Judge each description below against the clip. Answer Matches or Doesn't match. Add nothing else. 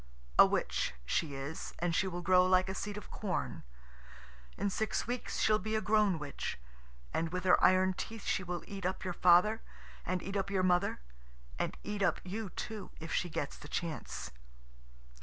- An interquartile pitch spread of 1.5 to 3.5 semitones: Matches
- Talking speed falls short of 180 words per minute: Doesn't match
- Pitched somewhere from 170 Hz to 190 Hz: Matches